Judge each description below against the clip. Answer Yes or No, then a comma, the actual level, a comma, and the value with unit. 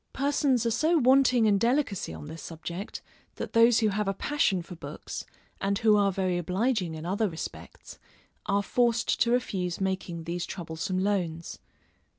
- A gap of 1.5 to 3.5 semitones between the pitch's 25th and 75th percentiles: No, average, 4.9 semitones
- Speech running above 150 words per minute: Yes, average, 160 wpm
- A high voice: Yes, high, 200 Hz